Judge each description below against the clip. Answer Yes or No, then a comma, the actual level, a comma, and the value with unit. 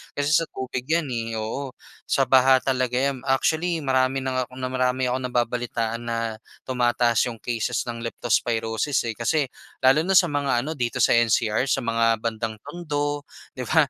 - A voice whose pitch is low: Yes, low, 130 Hz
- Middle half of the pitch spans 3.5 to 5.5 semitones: No, average, 2.9 semitones